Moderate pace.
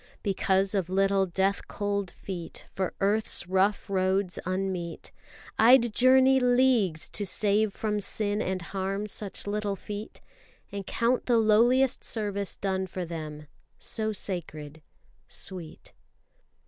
No: slow, 120 wpm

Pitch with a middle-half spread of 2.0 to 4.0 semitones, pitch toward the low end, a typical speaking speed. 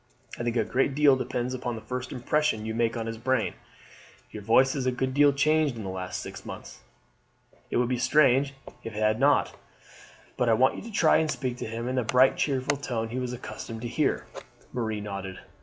No: average, 2.9 semitones; low, 125 Hz; fast, 220 wpm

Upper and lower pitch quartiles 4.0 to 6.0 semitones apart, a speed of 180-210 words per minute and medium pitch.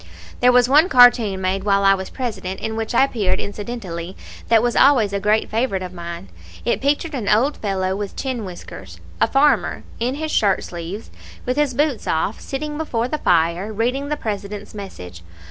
No: average, 5.1 semitones; average, 185 wpm; high, 215 Hz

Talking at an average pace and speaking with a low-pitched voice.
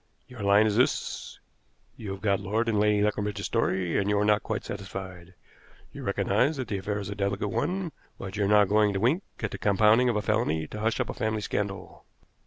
No: fast, 220 wpm; low, 105 Hz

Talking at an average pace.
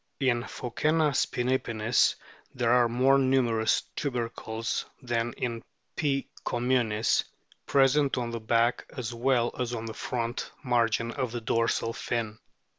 No: slow, 130 wpm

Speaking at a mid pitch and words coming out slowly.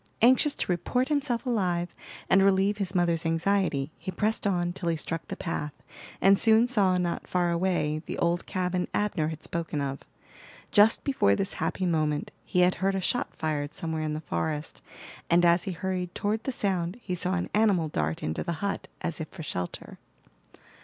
No: medium, 180 Hz; average, 185 wpm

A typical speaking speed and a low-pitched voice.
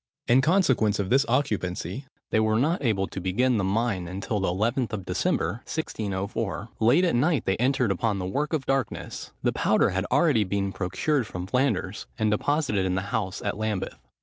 Yes: average, 185 wpm; low, 110 Hz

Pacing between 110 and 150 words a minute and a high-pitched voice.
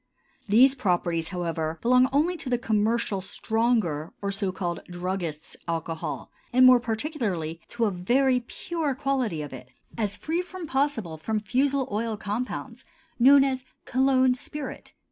Yes: average, 145 wpm; high, 225 Hz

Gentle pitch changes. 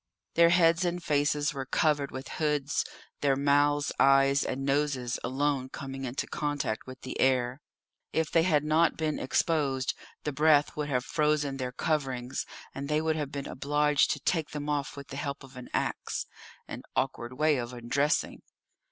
Yes: narrow, 2.1 semitones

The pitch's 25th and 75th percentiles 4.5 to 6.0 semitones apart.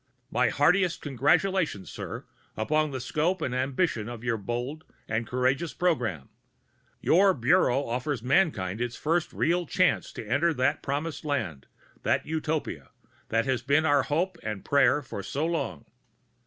Yes: average, 5.0 semitones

